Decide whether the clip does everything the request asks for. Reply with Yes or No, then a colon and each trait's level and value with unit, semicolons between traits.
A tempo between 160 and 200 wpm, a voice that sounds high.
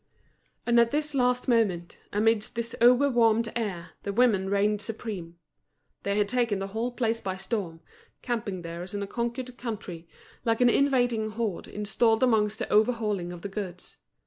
Yes: average, 170 wpm; high, 220 Hz